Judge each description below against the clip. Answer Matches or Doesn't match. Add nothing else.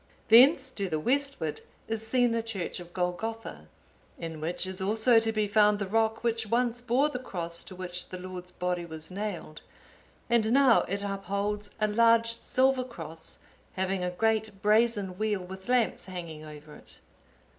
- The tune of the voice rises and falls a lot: Doesn't match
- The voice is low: Doesn't match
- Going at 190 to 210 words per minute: Doesn't match